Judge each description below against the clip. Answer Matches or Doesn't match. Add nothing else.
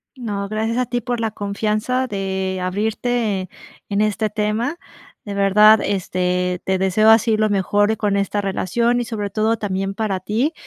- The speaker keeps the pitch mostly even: Matches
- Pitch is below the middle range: Doesn't match